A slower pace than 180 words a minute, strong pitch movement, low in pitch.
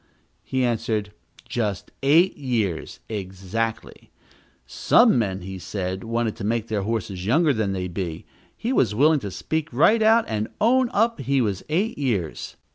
Yes: average, 155 wpm; wide, 6.9 semitones; low, 115 Hz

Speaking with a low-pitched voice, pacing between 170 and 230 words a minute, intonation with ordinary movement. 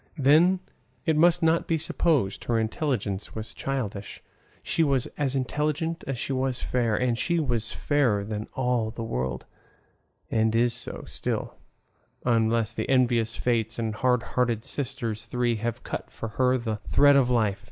No: low, 120 Hz; average, 160 wpm; average, 3.7 semitones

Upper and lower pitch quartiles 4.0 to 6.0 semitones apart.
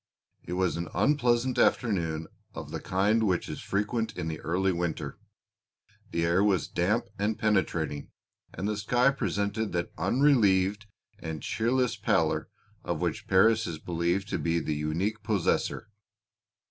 Yes: average, 4.5 semitones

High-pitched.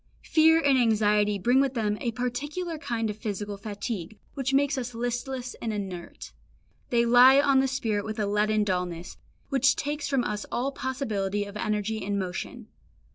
Yes: high, 230 Hz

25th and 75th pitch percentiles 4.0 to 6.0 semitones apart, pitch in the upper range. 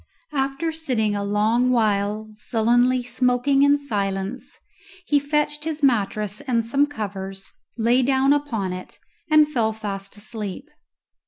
Yes: average, 4.9 semitones; high, 235 Hz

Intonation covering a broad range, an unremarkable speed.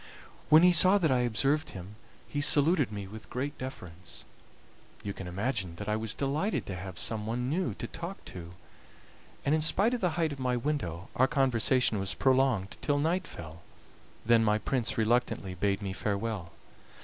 Yes: wide, 6.5 semitones; average, 180 wpm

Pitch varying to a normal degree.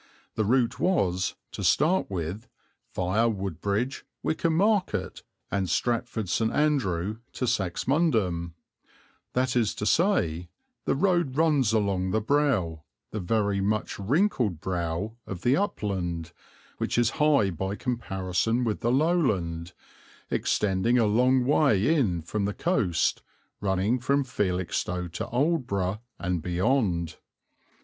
No: wide, 6.2 semitones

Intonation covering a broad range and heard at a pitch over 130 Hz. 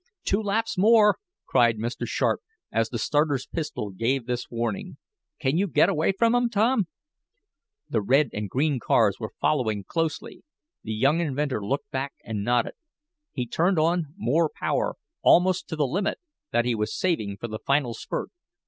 Yes: wide, 7.4 semitones; medium, 140 Hz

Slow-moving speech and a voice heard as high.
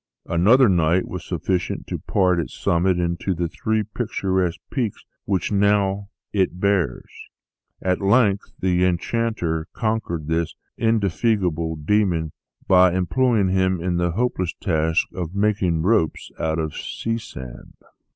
No: slow, 130 wpm; very low, 90 Hz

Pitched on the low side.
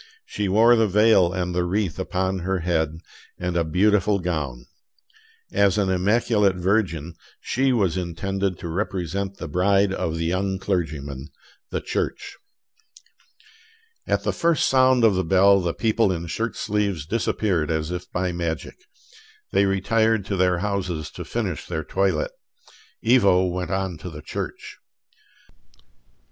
Yes: very low, 95 Hz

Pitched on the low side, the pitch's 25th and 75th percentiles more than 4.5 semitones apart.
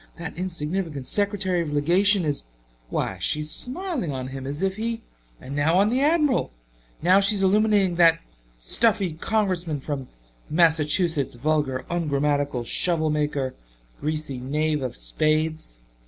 No: medium, 160 Hz; average, 4.9 semitones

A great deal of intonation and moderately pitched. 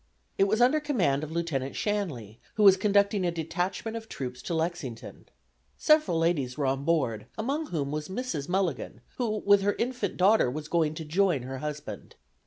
Yes: wide, 6.3 semitones; medium, 170 Hz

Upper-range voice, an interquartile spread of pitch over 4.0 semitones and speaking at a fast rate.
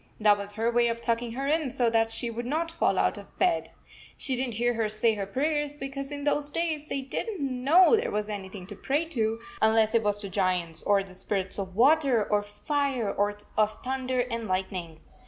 Yes: high, 235 Hz; average, 5.0 semitones; fast, 230 wpm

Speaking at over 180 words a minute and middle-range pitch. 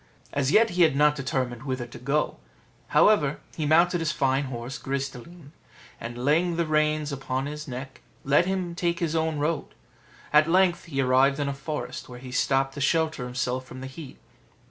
Yes: average, 190 wpm; medium, 145 Hz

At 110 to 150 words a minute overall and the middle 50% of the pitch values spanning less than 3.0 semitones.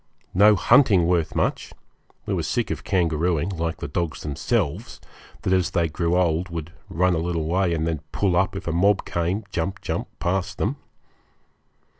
No: average, 175 wpm; narrow, 2.6 semitones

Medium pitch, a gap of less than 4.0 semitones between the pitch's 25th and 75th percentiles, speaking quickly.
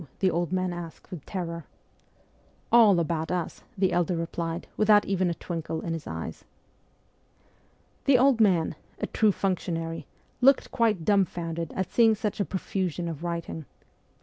No: medium, 175 Hz; average, 3.3 semitones; average, 150 wpm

